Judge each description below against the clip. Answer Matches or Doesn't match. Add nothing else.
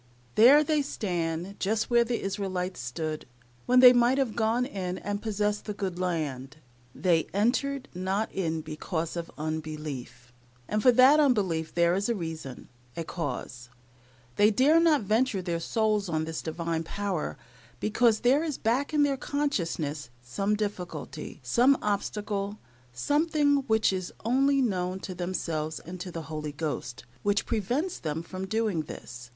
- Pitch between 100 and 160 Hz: Doesn't match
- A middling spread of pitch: Doesn't match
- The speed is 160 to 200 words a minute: Doesn't match